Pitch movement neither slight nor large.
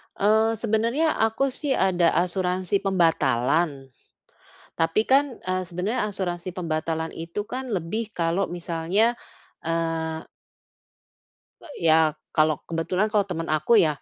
Yes: average, 4.7 semitones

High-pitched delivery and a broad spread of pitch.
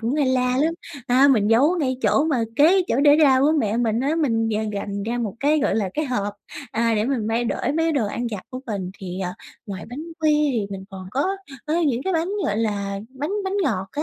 Yes: high, 245 Hz; wide, 5.8 semitones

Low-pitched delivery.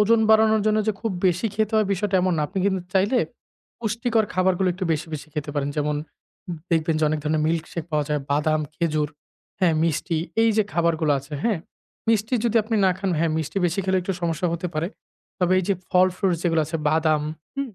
No: medium, 175 Hz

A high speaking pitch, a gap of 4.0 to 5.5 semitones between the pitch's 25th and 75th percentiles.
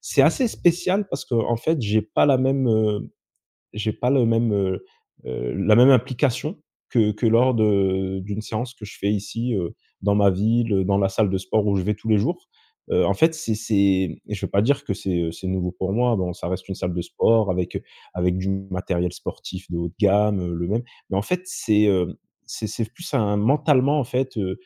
No: low, 105 Hz; average, 4.3 semitones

